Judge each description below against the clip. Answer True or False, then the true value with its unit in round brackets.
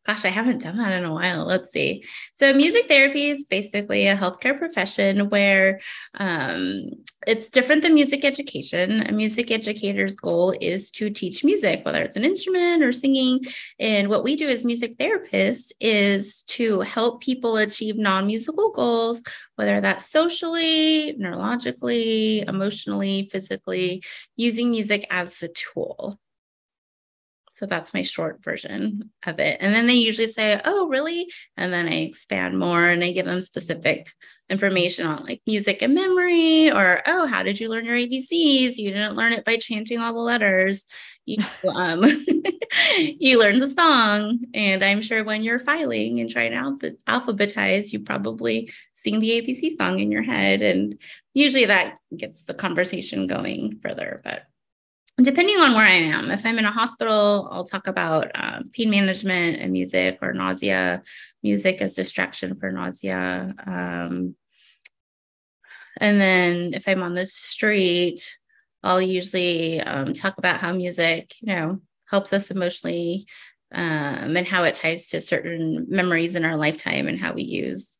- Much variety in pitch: True (5.8 semitones)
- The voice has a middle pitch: False (205 Hz)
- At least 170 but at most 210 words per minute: False (160 wpm)